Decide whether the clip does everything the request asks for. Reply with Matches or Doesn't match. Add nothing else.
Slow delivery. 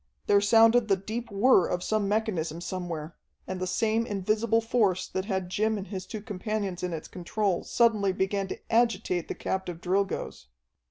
Doesn't match